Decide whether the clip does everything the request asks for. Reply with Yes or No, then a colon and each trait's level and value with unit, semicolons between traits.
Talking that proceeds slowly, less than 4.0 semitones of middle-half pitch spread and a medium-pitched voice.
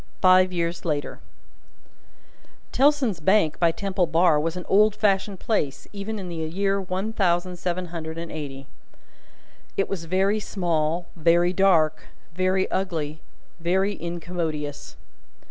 Yes: slow, 130 wpm; average, 2.9 semitones; medium, 180 Hz